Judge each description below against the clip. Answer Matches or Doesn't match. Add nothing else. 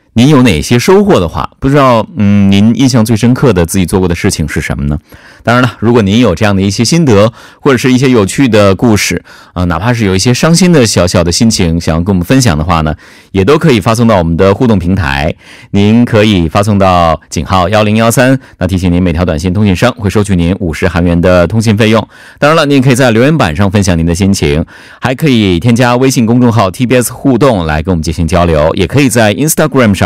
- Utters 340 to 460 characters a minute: Matches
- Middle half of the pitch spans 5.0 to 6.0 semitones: Matches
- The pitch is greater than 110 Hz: Doesn't match